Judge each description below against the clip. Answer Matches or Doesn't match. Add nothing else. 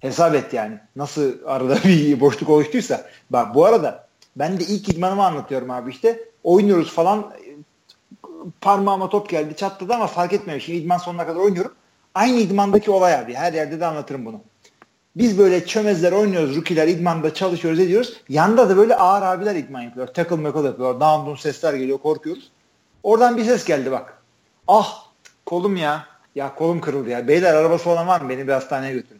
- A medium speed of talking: Doesn't match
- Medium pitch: Matches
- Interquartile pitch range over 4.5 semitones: Matches